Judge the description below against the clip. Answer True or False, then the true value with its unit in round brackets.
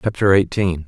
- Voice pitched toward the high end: False (95 Hz)